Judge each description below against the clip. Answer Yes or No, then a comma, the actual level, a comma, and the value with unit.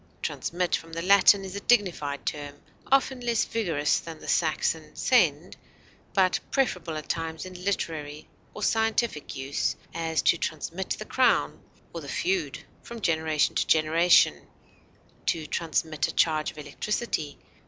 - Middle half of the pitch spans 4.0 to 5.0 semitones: Yes, average, 4.6 semitones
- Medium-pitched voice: Yes, medium, 165 Hz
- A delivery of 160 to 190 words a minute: No, average, 145 wpm